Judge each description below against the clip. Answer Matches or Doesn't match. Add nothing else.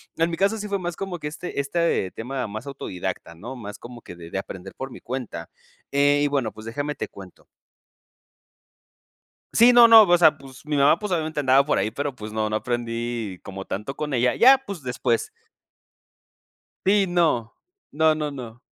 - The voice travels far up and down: Matches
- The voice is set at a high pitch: Doesn't match